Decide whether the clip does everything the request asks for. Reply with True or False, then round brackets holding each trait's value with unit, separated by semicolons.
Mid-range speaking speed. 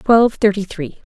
True (165 wpm)